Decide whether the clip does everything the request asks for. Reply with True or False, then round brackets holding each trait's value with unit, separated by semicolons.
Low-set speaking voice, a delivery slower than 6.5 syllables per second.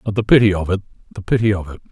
False (100 Hz; 8.1 syllables/s)